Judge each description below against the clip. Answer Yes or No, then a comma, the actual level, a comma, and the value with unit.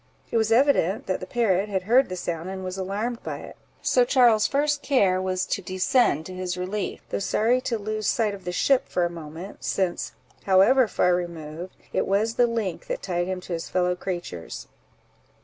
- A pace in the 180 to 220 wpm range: Yes, average, 200 wpm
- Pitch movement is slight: No, average, 4.0 semitones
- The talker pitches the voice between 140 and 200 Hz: Yes, high, 190 Hz